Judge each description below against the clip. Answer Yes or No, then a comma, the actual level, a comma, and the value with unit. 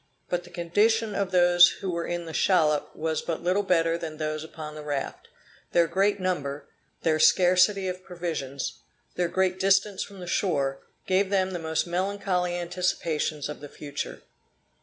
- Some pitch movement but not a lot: Yes, average, 3.0 semitones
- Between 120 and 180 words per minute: Yes, average, 165 wpm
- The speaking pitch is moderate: Yes, medium, 175 Hz